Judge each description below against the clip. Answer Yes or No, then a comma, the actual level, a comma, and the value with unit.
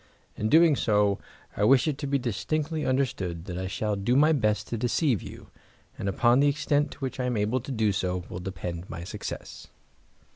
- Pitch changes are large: Yes, wide, 5.9 semitones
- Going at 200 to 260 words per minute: Yes, fast, 205 wpm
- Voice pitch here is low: Yes, low, 120 Hz